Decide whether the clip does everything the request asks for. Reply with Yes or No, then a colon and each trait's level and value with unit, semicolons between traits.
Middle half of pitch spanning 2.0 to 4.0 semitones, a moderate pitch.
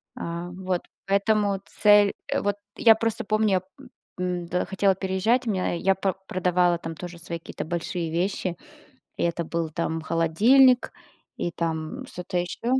Yes: average, 3.2 semitones; medium, 180 Hz